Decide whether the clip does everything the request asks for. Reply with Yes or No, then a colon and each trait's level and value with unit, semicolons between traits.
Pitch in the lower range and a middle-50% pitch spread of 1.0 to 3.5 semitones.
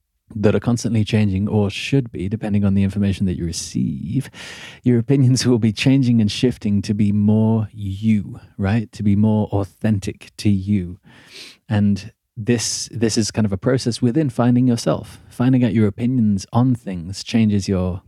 Yes: low, 110 Hz; average, 2.9 semitones